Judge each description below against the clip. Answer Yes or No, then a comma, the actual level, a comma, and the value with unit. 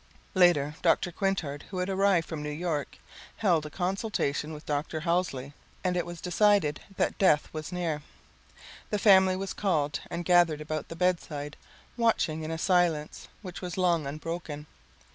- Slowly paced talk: No, average, 160 wpm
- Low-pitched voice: No, medium, 170 Hz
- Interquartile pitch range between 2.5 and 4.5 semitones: Yes, average, 3.3 semitones